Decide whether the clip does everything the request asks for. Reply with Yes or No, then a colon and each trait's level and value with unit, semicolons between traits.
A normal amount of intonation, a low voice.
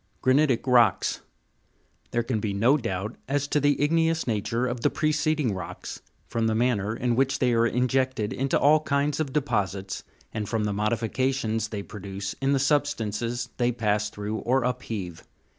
Yes: average, 4.1 semitones; low, 120 Hz